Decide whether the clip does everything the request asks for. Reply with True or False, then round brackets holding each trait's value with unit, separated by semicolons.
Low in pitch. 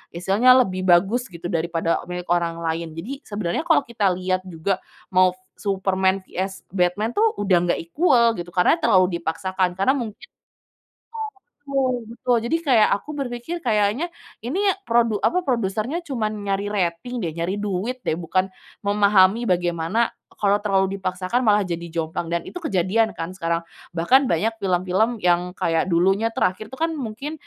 False (195 Hz)